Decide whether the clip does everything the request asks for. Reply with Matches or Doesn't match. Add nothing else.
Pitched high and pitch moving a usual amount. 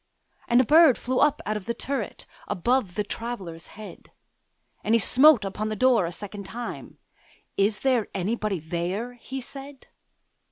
Matches